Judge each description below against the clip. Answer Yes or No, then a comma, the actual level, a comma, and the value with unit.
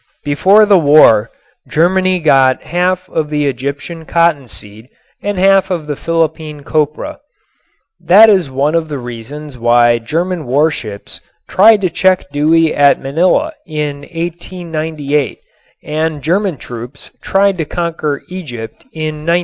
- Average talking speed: No, slow, 130 wpm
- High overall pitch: No, medium, 155 Hz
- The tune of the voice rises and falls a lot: No, average, 3.9 semitones